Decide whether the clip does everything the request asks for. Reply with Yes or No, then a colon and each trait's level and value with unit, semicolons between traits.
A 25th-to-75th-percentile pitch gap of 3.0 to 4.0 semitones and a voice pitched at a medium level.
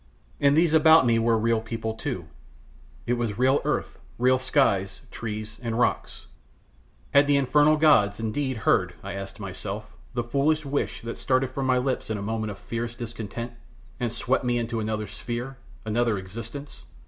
No: average, 3.4 semitones; low, 120 Hz